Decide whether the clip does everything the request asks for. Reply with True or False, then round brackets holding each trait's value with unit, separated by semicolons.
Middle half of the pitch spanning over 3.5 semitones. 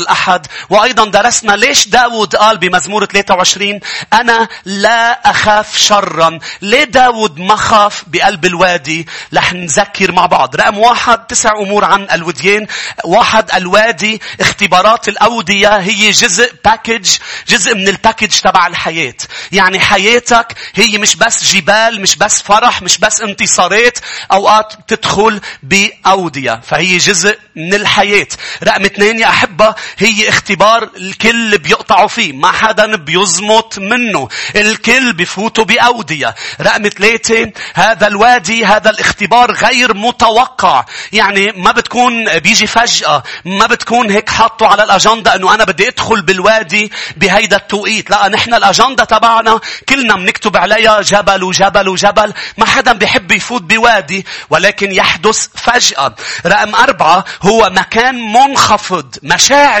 False (2.4 semitones)